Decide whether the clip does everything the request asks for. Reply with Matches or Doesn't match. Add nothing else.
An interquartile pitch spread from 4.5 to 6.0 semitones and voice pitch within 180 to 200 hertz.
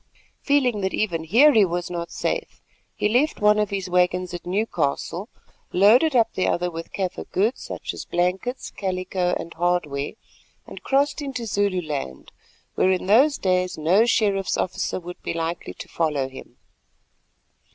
Doesn't match